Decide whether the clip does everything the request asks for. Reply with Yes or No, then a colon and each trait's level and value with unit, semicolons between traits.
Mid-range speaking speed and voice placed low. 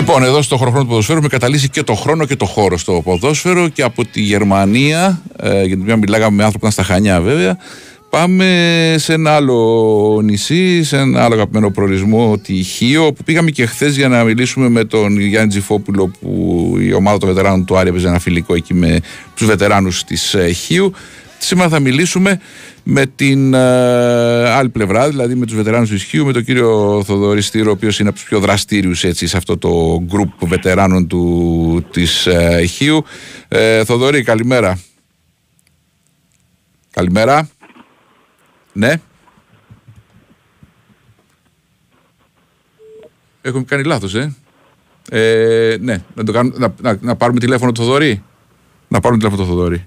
Yes: average, 155 wpm; low, 115 Hz